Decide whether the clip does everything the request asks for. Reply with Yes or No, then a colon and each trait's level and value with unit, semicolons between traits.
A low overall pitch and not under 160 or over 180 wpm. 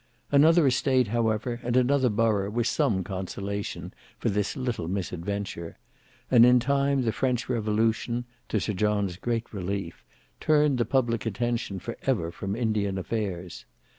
No: low, 110 Hz; average, 140 wpm